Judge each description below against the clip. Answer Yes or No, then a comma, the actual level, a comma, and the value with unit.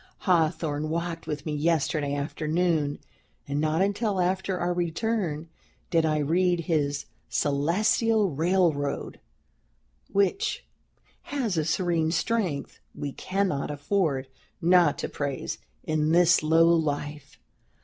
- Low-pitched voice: No, medium, 165 Hz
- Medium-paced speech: No, slow, 110 wpm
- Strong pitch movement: No, average, 3.6 semitones